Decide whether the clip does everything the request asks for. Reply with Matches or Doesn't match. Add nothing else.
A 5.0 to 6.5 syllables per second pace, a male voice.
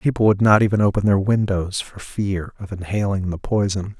Matches